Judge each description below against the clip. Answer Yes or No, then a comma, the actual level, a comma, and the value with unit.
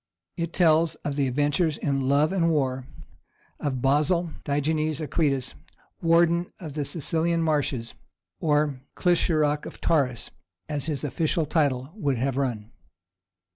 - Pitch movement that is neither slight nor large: Yes, average, 3.1 semitones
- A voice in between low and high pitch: Yes, medium, 150 Hz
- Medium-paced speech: No, slow, 130 wpm